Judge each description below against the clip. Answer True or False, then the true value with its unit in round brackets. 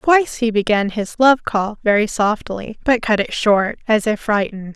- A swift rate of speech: False (190 wpm)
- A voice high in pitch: True (220 Hz)